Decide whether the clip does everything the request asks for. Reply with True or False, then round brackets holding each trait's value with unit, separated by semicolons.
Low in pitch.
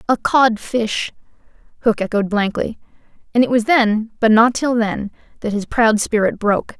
False (225 Hz)